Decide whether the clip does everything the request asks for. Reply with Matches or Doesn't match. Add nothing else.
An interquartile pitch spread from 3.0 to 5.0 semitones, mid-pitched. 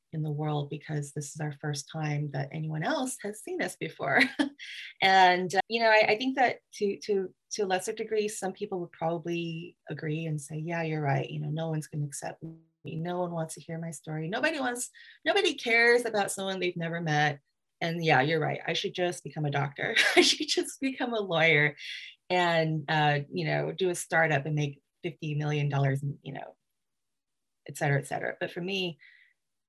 Matches